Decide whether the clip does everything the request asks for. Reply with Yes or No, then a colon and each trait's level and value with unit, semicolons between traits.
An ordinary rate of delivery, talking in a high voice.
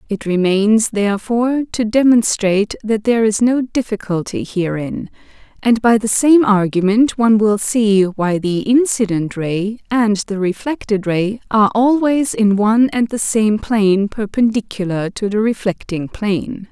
Yes: average, 145 wpm; high, 215 Hz